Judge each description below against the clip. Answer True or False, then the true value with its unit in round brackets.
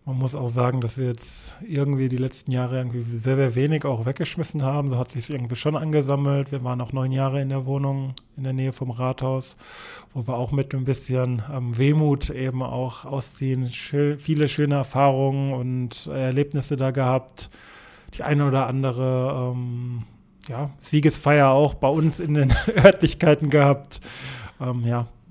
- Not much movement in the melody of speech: True (2.0 semitones)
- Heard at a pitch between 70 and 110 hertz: False (135 Hz)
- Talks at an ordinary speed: True (175 wpm)